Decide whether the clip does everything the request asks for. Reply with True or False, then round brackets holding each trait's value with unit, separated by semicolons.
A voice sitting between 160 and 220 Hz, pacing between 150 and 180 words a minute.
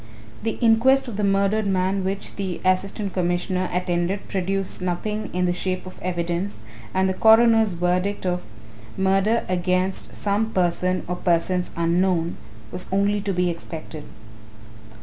False (185 Hz; 140 wpm)